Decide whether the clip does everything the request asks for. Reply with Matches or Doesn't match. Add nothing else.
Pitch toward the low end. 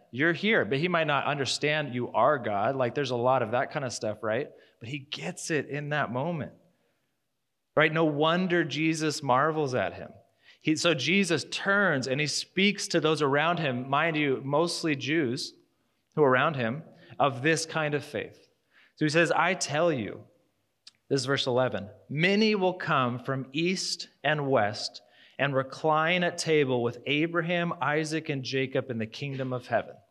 Doesn't match